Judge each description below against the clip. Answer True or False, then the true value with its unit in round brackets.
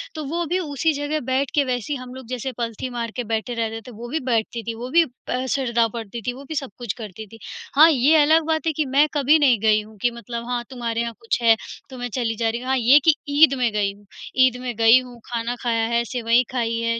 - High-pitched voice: True (245 Hz)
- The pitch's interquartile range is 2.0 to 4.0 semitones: True (3.1 semitones)